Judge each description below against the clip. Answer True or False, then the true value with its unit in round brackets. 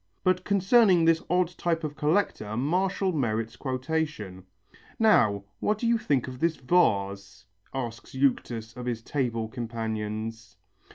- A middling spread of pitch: False (7.5 semitones)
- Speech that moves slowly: True (130 wpm)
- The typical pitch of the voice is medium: False (130 Hz)